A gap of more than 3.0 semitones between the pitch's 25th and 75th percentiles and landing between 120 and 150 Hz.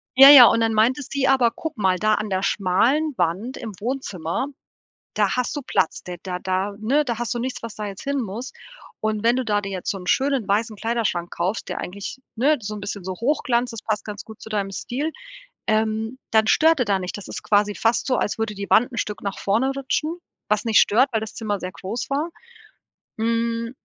No: average, 3.8 semitones; high, 220 Hz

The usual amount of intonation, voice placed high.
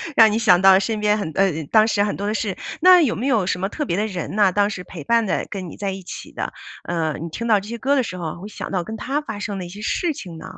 Yes: average, 3.4 semitones; high, 205 Hz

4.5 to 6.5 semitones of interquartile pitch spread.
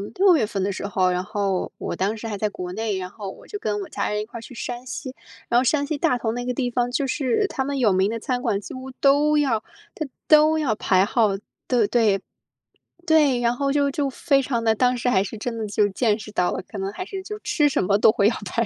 Yes: average, 4.9 semitones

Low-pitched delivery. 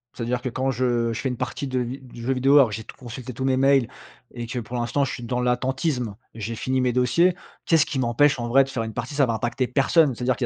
Yes: low, 125 Hz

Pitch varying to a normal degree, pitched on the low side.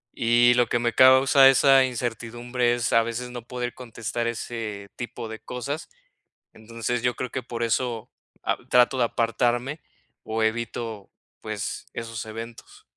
No: narrow, 1.5 semitones; low, 120 Hz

